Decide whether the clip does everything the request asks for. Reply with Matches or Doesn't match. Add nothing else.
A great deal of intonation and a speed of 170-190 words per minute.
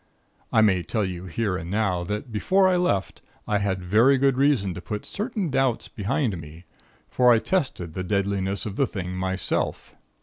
Matches